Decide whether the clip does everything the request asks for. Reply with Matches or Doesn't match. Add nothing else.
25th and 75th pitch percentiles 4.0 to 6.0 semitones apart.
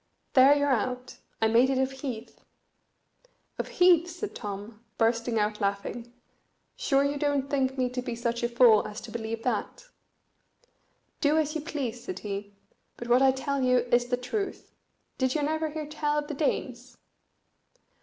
Doesn't match